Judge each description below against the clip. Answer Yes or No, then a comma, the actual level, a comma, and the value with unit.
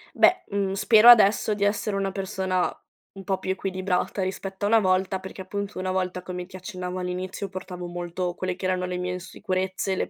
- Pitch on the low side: No, high, 190 Hz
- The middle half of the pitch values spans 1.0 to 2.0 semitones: Yes, narrow, 1.3 semitones